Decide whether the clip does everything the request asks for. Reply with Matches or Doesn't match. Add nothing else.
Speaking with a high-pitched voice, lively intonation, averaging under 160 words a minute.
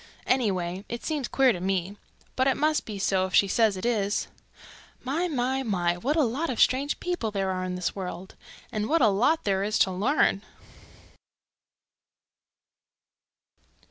Doesn't match